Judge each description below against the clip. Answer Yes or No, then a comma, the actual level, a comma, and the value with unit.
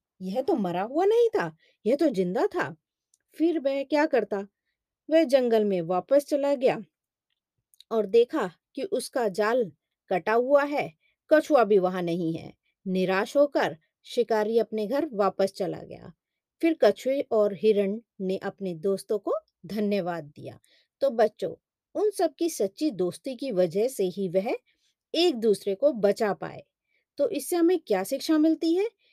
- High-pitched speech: Yes, high, 220 Hz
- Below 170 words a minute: Yes, average, 155 wpm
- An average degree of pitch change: No, wide, 7.5 semitones